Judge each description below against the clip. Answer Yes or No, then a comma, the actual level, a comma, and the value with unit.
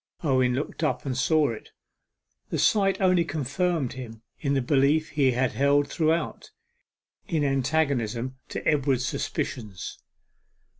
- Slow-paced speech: Yes, slow, 130 wpm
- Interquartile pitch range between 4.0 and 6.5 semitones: No, average, 3.5 semitones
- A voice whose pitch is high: No, medium, 140 Hz